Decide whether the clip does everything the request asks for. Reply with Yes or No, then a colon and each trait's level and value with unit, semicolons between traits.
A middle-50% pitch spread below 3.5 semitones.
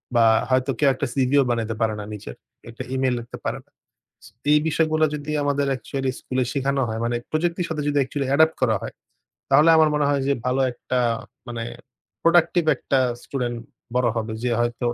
No: average, 3.8 semitones